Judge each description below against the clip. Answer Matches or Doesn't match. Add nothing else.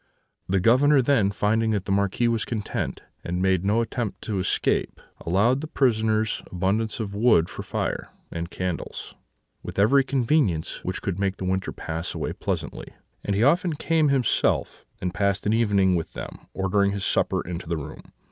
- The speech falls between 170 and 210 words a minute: Matches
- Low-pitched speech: Matches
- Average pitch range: Matches